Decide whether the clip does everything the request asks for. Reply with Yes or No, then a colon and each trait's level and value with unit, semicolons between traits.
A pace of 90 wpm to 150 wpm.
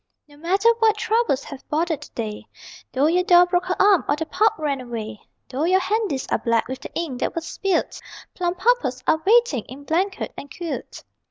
No: average, 195 wpm